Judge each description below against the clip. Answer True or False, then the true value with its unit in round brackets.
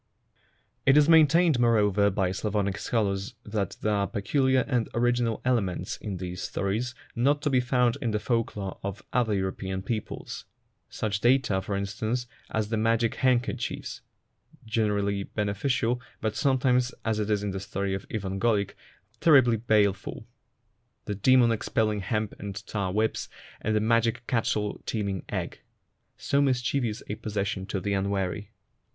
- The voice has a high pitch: False (110 Hz)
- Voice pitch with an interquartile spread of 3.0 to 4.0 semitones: True (3.5 semitones)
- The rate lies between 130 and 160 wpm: True (145 wpm)